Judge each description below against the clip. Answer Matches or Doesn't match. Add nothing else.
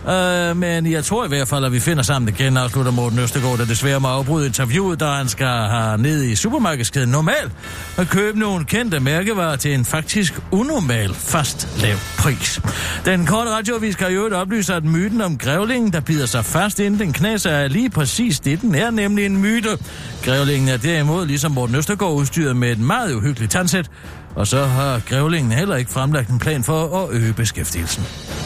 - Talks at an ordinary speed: Matches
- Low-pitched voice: Doesn't match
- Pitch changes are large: Matches